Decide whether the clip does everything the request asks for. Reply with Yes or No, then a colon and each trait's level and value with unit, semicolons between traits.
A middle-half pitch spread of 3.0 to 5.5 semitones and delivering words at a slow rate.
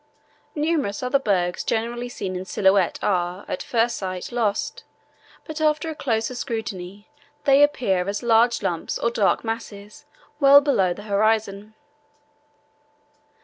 Yes: average, 4.2 semitones; slow, 130 wpm